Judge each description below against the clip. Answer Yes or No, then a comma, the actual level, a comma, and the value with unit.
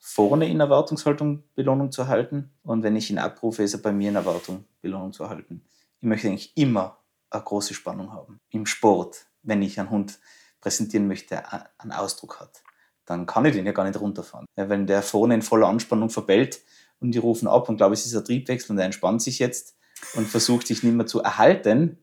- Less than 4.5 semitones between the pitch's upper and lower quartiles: Yes, average, 3.7 semitones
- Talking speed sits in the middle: No, fast, 210 wpm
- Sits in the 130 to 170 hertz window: No, low, 110 Hz